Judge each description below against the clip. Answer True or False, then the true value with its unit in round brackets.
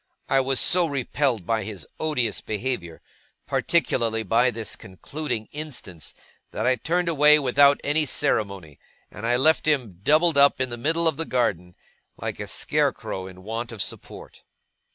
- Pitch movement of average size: False (5.7 semitones)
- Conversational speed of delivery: True (155 wpm)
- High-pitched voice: False (125 Hz)